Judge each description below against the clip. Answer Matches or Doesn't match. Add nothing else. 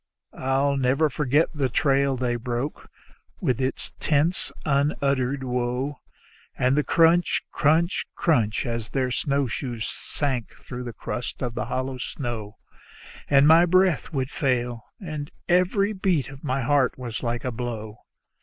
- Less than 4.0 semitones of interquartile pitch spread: Matches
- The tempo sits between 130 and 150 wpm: Matches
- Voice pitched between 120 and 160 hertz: Matches